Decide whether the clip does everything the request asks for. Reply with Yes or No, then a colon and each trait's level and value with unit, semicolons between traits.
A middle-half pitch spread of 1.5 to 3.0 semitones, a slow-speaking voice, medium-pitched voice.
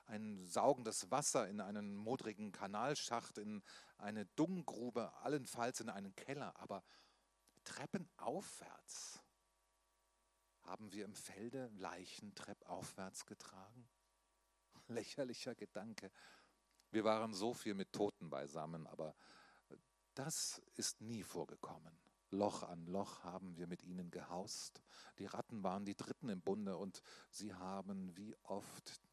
No: narrow, 2.4 semitones; slow, 120 wpm; low, 100 Hz